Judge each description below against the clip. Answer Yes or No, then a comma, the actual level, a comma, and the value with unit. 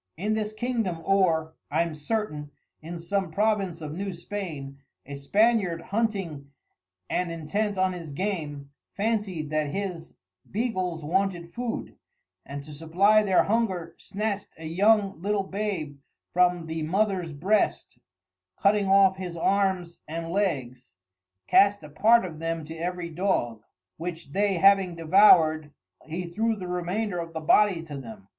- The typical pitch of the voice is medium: Yes, medium, 180 Hz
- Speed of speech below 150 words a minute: Yes, average, 140 wpm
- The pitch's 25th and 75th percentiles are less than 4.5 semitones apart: Yes, average, 4.0 semitones